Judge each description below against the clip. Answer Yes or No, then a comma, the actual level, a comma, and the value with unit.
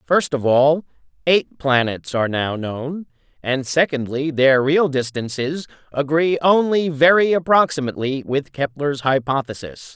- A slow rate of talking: Yes, slow, 120 wpm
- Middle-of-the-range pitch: Yes, medium, 145 Hz